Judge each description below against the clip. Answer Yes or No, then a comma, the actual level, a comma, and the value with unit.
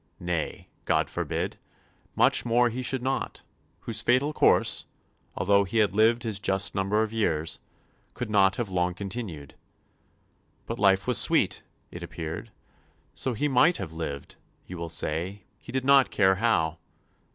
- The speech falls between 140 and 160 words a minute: Yes, average, 150 wpm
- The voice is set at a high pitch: No, low, 100 Hz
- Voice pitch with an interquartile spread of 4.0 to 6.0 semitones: Yes, average, 5.1 semitones